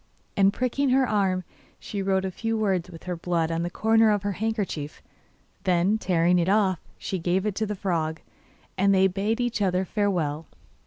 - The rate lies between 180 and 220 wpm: Yes, average, 190 wpm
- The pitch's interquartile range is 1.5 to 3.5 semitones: Yes, average, 3.1 semitones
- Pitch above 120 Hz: Yes, high, 190 Hz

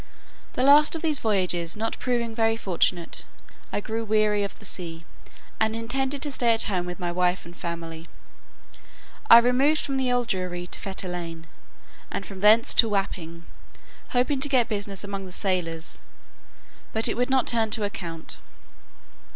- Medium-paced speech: Yes, average, 165 wpm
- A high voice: Yes, high, 210 Hz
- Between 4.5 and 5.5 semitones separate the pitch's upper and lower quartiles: Yes, average, 5.2 semitones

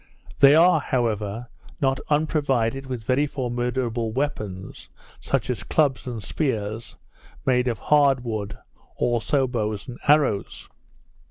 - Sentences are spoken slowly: Yes, slow, 115 wpm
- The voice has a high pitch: No, low, 125 Hz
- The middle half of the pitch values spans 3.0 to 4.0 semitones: Yes, average, 3.7 semitones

